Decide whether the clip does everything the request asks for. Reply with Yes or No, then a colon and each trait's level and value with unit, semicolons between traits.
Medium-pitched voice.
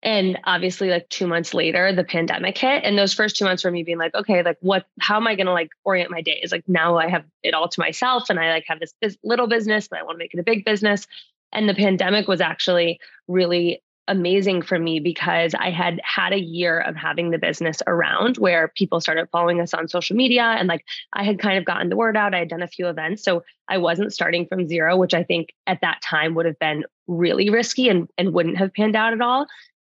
Yes: medium, 180 Hz